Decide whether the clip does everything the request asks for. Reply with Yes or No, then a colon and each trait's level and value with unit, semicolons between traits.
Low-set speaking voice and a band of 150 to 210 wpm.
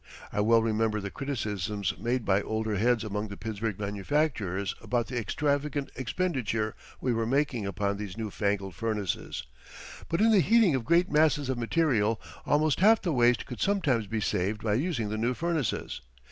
Yes: low, 115 Hz; average, 175 wpm